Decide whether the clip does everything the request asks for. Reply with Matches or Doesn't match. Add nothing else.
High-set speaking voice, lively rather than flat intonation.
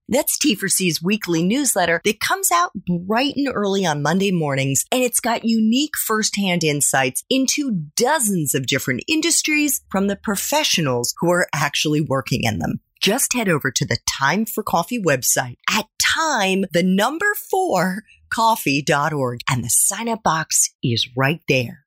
Matches